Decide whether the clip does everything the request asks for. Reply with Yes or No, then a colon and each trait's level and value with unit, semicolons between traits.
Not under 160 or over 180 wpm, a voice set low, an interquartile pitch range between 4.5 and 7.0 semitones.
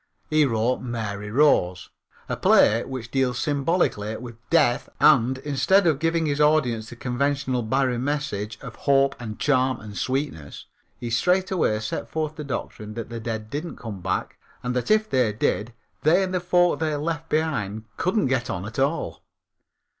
Yes: average, 170 wpm; low, 130 Hz; average, 5.2 semitones